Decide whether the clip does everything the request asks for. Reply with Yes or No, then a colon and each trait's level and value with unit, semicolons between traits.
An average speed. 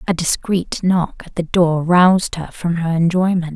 Yes: average, 185 wpm